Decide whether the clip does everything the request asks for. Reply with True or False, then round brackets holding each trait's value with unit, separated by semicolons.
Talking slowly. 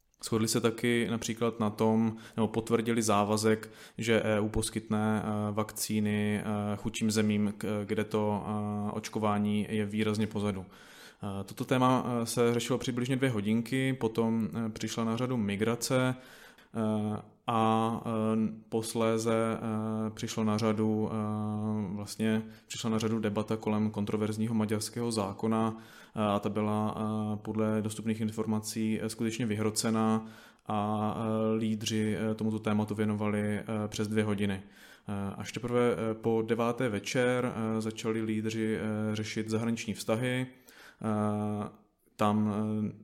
True (105 wpm)